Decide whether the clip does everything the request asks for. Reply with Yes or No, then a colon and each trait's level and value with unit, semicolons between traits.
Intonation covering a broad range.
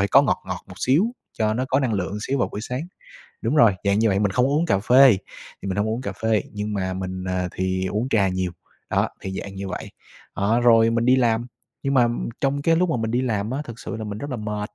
No: average, 4.5 semitones